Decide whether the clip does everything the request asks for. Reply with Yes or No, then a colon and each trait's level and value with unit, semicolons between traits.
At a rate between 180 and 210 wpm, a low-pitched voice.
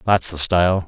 Yes: fast, 205 wpm; very low, 90 Hz